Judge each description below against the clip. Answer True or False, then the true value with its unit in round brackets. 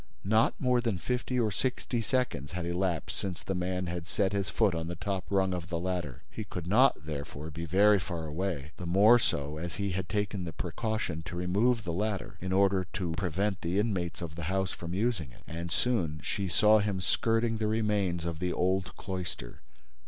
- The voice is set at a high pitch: False (95 Hz)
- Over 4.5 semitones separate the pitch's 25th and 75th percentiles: False (3.5 semitones)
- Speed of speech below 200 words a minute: False (205 wpm)